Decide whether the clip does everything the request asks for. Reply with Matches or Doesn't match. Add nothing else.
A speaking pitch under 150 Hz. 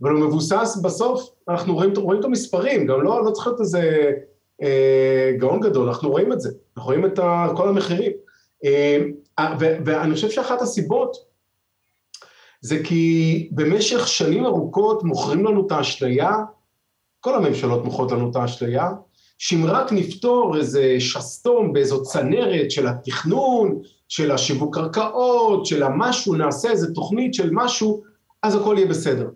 Doesn't match